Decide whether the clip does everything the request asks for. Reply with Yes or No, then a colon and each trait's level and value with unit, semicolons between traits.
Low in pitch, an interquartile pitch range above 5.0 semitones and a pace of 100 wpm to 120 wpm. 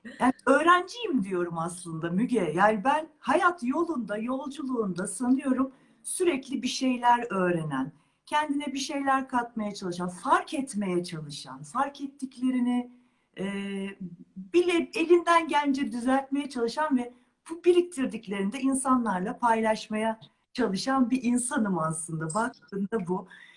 No: high, 245 Hz; wide, 5.6 semitones; average, 105 wpm